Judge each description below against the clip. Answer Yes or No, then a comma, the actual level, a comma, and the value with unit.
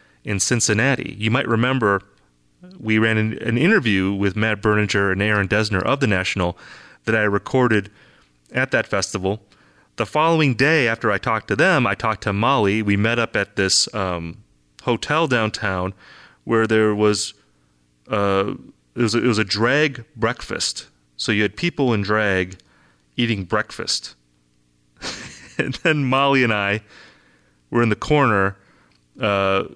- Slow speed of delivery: No, average, 150 wpm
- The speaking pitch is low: Yes, low, 105 Hz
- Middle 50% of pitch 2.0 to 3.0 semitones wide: No, average, 3.6 semitones